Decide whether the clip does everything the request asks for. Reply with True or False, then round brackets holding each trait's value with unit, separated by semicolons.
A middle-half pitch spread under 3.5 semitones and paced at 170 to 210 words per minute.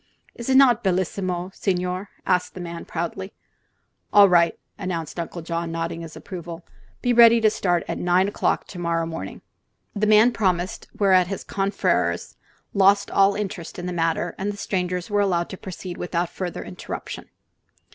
False (2.7 semitones; 155 wpm)